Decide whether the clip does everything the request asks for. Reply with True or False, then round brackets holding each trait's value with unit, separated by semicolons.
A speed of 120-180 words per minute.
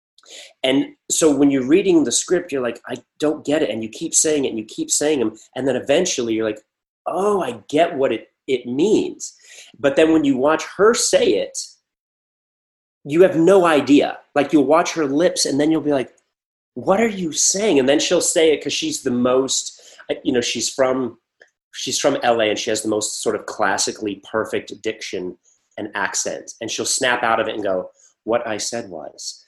False (205 wpm)